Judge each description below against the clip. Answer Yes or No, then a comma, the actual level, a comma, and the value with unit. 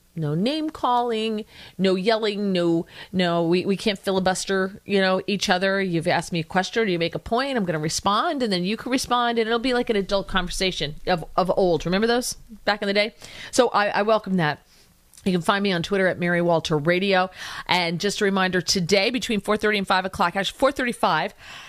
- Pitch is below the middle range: No, high, 195 Hz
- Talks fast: Yes, fast, 215 wpm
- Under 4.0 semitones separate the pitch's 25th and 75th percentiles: Yes, average, 3.5 semitones